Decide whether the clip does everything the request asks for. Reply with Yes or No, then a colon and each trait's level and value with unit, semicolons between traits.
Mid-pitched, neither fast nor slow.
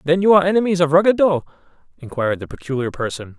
Yes: medium, 160 Hz; average, 175 wpm